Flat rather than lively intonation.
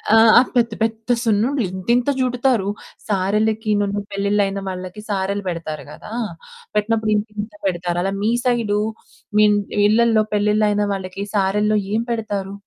Yes: narrow, 2.2 semitones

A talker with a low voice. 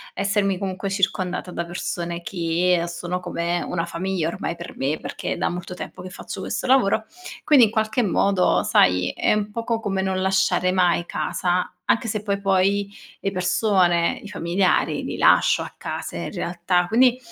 No: medium, 185 Hz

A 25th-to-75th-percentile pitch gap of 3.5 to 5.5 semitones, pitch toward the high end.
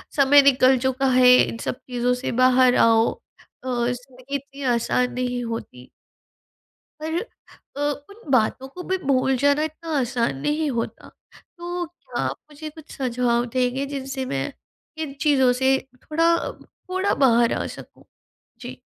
No: average, 2.9 semitones; very high, 265 Hz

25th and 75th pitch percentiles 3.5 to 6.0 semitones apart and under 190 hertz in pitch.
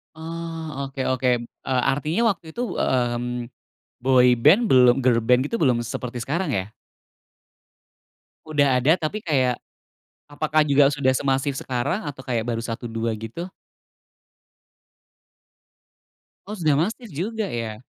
Yes: average, 4.6 semitones; low, 135 Hz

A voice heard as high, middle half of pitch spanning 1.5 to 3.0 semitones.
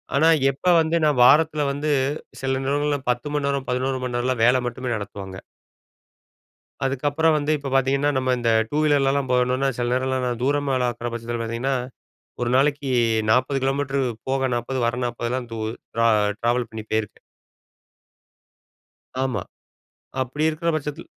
No: low, 130 Hz; average, 2.7 semitones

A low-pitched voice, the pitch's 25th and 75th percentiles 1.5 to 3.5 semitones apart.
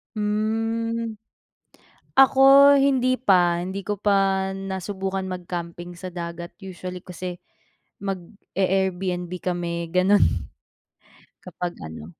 No: high, 190 Hz; average, 2.7 semitones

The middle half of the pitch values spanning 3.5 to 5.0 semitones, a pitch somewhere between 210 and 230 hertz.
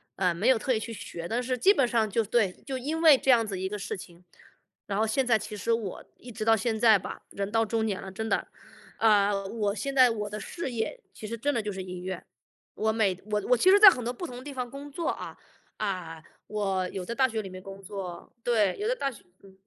Yes: average, 4.1 semitones; high, 220 Hz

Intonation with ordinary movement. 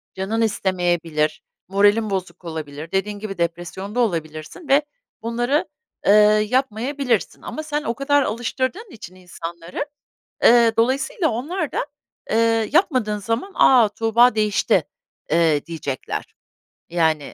No: wide, 6.2 semitones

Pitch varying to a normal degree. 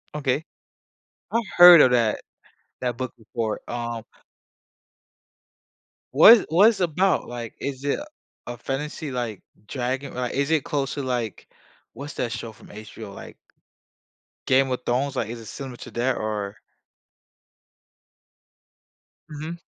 Yes: average, 3.7 semitones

